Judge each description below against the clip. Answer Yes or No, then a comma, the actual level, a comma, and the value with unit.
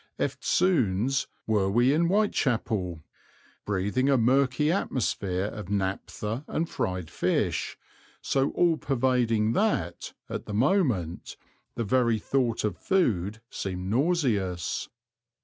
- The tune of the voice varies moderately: No, wide, 5.8 semitones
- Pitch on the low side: Yes, low, 115 Hz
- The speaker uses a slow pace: Yes, slow, 110 wpm